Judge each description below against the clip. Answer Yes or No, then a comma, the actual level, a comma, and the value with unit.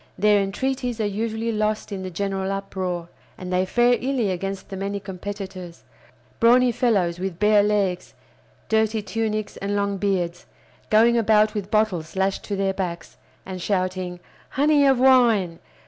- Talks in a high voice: Yes, high, 200 Hz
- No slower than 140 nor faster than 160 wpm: Yes, average, 150 wpm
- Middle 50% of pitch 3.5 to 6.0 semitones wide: No, average, 2.8 semitones